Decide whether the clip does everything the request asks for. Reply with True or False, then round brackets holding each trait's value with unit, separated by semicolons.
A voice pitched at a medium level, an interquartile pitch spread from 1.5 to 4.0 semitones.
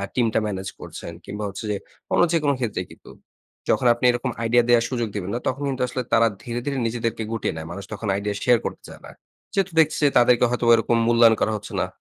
False (115 Hz; 2.8 semitones)